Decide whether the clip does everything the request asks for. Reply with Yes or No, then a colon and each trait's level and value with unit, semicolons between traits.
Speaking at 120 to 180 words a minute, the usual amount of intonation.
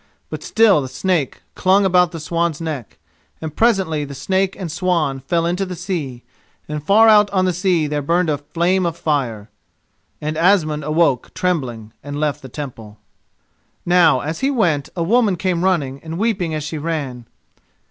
Yes: average, 170 wpm; average, 4.1 semitones